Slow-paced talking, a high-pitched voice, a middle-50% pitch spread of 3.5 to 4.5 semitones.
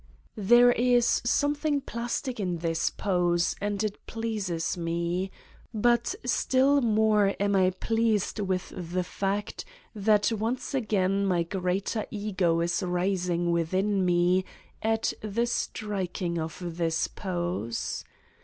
Yes: slow, 120 wpm; high, 195 Hz; average, 4.0 semitones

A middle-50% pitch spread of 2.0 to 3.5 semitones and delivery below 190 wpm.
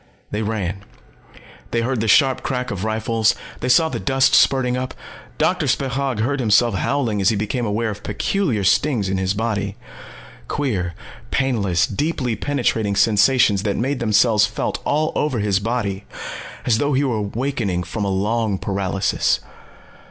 No: average, 4.2 semitones; average, 155 wpm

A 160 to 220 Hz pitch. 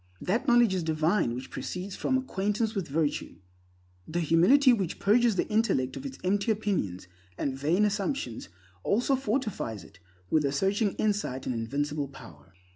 Yes: high, 190 Hz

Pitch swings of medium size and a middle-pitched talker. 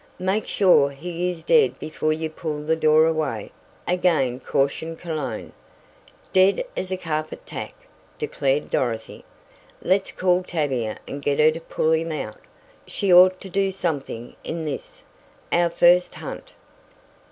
Yes: average, 3.5 semitones; medium, 160 Hz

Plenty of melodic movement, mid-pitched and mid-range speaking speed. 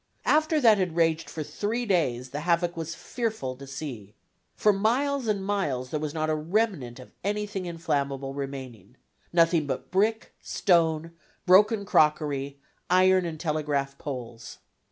Yes: wide, 6.2 semitones; medium, 165 Hz; average, 145 wpm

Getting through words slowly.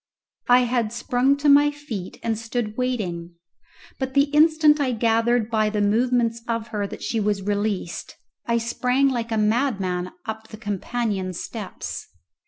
No: average, 155 wpm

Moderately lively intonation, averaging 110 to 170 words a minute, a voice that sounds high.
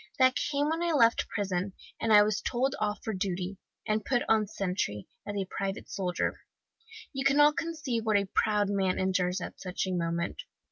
No: average, 4.6 semitones; average, 185 wpm; high, 205 Hz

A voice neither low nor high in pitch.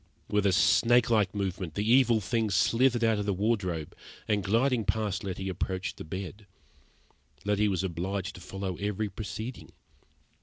No: low, 100 Hz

